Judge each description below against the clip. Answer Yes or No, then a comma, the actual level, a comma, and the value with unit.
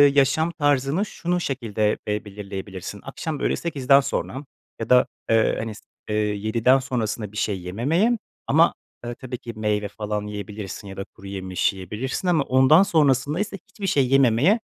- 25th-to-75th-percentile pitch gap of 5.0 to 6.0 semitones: Yes, wide, 5.5 semitones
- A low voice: Yes, low, 120 Hz